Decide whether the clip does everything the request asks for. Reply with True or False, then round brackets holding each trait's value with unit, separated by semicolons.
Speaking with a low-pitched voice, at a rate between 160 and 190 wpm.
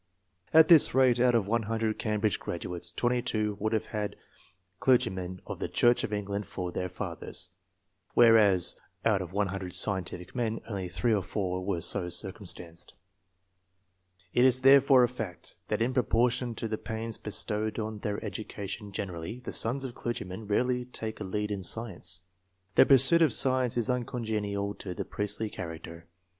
True (110 Hz; 165 wpm)